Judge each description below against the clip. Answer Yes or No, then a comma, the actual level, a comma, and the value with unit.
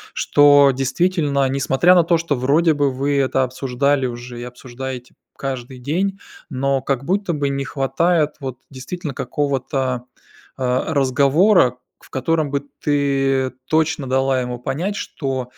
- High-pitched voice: No, low, 135 Hz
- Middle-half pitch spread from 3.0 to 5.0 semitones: No, narrow, 2.5 semitones